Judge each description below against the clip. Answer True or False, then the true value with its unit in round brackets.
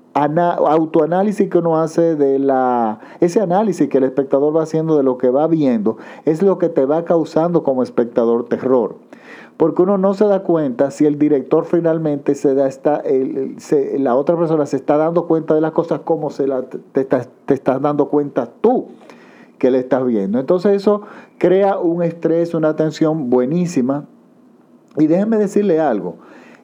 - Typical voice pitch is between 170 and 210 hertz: False (155 Hz)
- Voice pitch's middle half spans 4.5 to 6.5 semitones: False (3.6 semitones)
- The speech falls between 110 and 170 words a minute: False (180 wpm)